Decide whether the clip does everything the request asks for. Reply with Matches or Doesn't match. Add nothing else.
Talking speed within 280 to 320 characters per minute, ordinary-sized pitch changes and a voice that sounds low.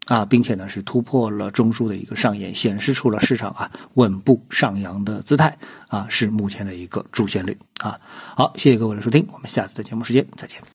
Doesn't match